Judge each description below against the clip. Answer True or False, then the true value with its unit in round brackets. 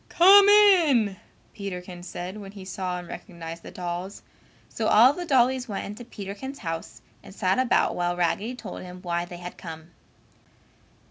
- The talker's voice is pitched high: True (195 Hz)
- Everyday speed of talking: True (160 wpm)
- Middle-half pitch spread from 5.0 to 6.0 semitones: True (5.6 semitones)